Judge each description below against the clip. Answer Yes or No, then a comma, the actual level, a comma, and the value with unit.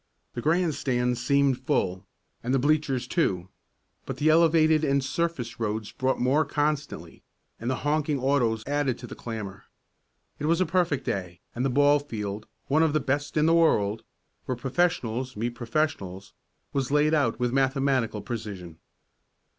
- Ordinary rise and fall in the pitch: Yes, average, 4.6 semitones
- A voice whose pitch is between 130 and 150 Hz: Yes, low, 135 Hz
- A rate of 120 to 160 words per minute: Yes, average, 155 wpm